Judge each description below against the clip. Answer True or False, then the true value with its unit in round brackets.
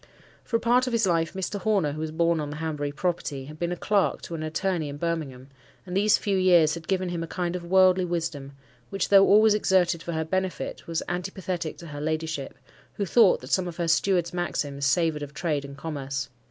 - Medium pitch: True (170 Hz)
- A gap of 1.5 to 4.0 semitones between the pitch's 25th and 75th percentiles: True (3.3 semitones)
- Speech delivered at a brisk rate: True (220 wpm)